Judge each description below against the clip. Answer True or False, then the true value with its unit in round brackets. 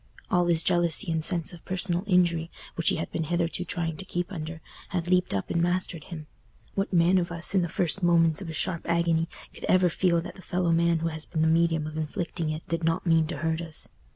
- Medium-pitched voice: True (170 Hz)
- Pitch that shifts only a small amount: True (1.6 semitones)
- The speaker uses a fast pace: True (235 wpm)